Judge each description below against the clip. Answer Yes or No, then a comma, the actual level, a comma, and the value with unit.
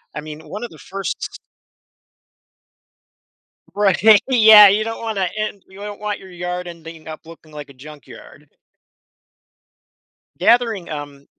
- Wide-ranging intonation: No, average, 5.0 semitones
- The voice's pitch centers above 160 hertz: Yes, medium, 185 Hz